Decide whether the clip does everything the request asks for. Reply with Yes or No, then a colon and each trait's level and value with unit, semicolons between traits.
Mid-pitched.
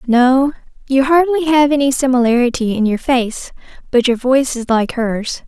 No: very high, 255 Hz